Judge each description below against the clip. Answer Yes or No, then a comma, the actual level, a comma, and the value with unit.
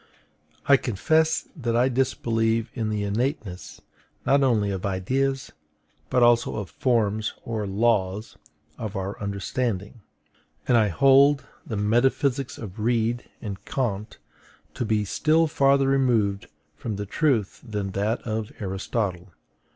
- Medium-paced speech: No, slow, 130 wpm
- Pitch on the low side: Yes, low, 115 Hz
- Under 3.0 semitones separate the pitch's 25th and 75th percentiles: No, average, 4.2 semitones